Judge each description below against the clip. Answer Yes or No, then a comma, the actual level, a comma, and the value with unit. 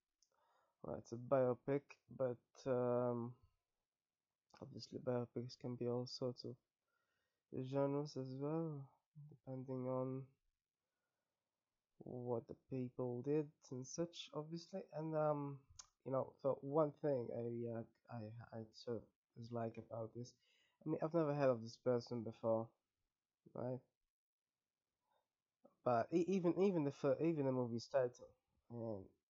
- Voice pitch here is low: Yes, low, 130 Hz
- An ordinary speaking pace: No, slow, 125 wpm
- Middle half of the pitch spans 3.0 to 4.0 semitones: Yes, average, 3.7 semitones